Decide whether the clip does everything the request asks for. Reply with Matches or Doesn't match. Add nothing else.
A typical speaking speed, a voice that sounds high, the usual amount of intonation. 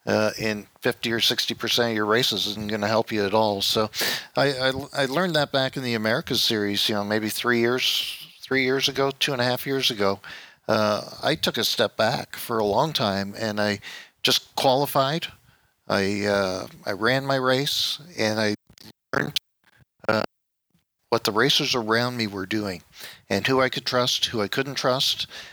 Doesn't match